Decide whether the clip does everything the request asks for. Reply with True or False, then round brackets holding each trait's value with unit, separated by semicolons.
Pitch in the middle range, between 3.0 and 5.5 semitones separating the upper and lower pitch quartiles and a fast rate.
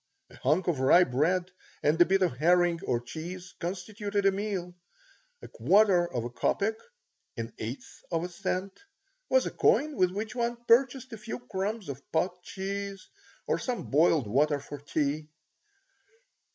False (180 Hz; 4.9 semitones; 160 wpm)